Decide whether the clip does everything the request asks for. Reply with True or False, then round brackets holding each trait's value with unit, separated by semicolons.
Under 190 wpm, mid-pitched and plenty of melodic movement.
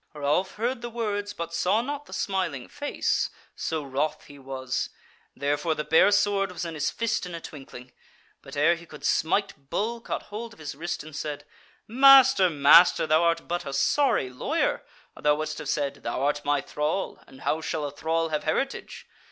False (195 wpm; 160 Hz; 5.8 semitones)